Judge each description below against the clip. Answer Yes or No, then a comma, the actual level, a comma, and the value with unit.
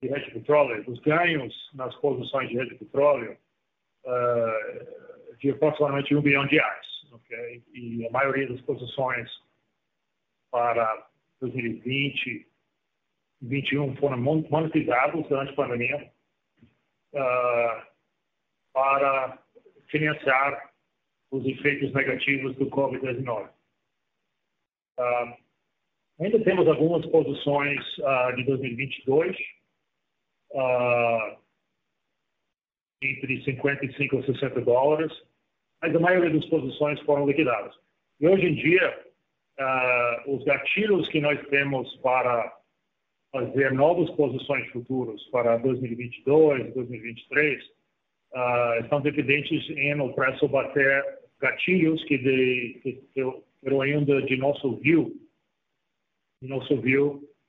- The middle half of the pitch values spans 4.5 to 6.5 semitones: No, narrow, 2.6 semitones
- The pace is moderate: No, slow, 100 wpm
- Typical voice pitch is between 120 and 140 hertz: Yes, low, 135 Hz